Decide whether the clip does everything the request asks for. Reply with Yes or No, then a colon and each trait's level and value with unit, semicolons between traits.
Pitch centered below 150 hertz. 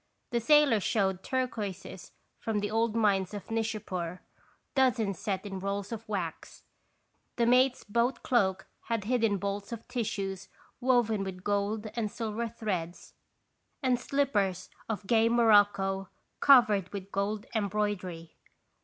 No: high, 210 Hz